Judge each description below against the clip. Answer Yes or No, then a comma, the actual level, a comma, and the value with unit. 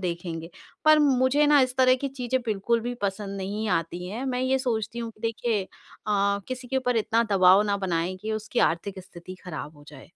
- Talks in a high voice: Yes, high, 215 Hz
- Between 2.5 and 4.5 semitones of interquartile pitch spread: No, average, 5.1 semitones